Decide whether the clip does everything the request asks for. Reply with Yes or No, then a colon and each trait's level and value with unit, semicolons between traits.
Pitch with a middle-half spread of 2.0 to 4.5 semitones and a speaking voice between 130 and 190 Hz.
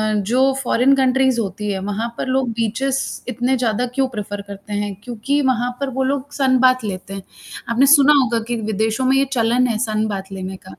No: average, 3.9 semitones; high, 240 Hz